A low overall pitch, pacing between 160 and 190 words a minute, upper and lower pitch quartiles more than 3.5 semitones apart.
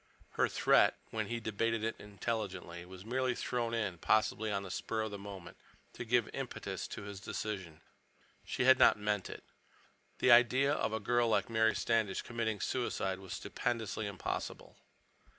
No: low, 110 Hz; average, 165 wpm; average, 2.9 semitones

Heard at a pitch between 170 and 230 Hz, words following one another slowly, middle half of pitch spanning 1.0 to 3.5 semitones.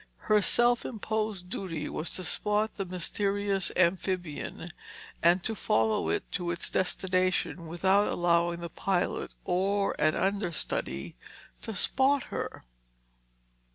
Yes: medium, 185 Hz; slow, 120 wpm; average, 2.9 semitones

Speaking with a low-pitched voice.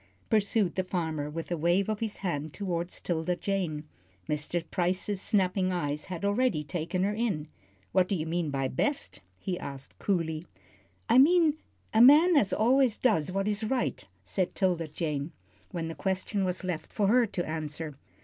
No: medium, 185 Hz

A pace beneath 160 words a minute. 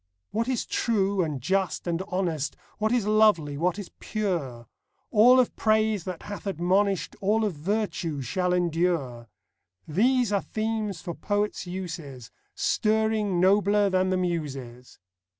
Yes: average, 145 wpm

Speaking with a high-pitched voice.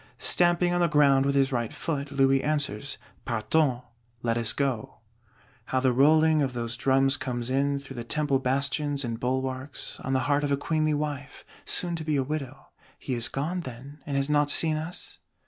No: medium, 140 Hz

